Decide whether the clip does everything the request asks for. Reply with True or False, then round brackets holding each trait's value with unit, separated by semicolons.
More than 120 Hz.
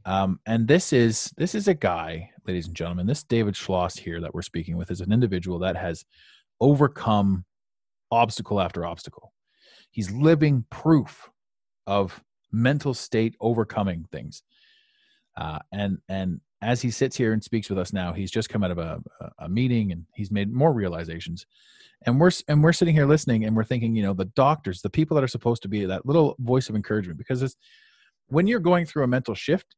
False (110 Hz)